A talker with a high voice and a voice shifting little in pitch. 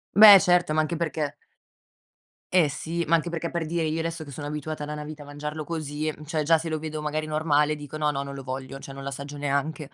No: medium, 155 Hz; narrow, 1.7 semitones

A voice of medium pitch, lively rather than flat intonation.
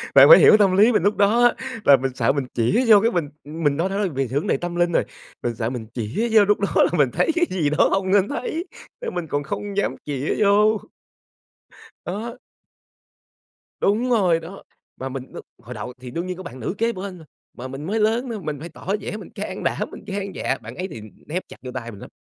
Yes: medium, 180 Hz; wide, 6.9 semitones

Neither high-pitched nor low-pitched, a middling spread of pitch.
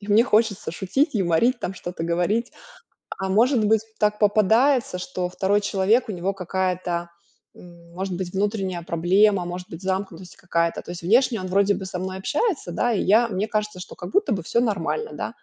No: high, 195 Hz; average, 3.2 semitones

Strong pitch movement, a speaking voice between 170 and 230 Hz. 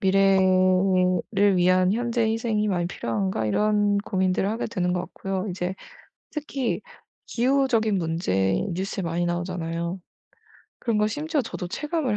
No: average, 3.6 semitones; high, 190 Hz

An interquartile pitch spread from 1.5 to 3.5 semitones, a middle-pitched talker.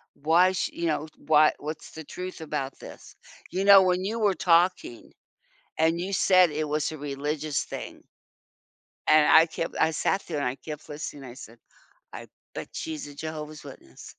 Yes: average, 3.1 semitones; medium, 155 Hz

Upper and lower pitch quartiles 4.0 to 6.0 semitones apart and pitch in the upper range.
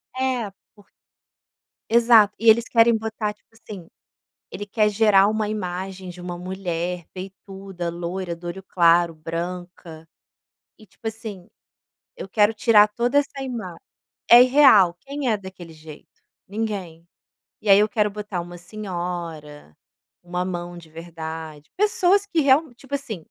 Yes: average, 4.3 semitones; high, 195 Hz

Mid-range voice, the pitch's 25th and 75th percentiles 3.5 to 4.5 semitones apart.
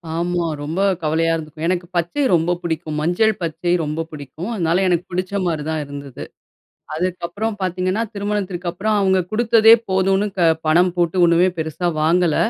No: medium, 175 Hz; average, 2.8 semitones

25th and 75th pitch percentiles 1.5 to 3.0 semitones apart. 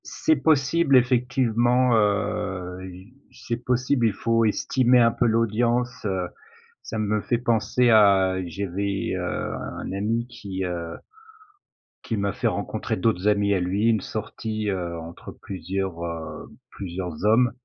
No: average, 4.1 semitones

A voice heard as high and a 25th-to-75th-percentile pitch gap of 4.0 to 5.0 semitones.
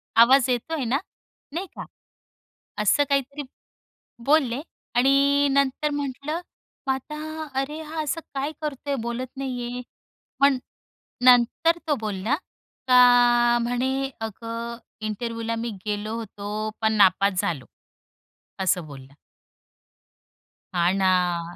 Yes: high, 245 Hz; average, 4.3 semitones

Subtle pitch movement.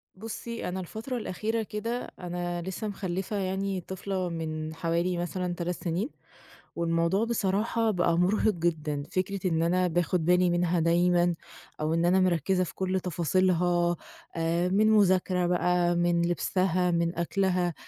Yes: narrow, 1.8 semitones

